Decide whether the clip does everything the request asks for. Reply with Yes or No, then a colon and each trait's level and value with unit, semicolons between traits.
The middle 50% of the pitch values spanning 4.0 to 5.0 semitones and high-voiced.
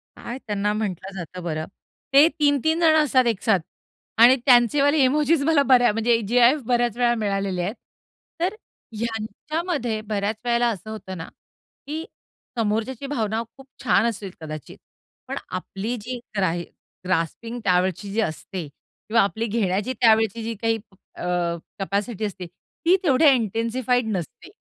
Yes: average, 4.3 semitones; high, 225 Hz